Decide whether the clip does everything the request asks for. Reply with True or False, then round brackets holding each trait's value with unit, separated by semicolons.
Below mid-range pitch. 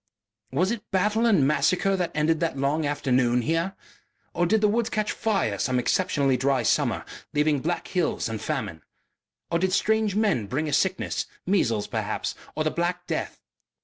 False (165 Hz)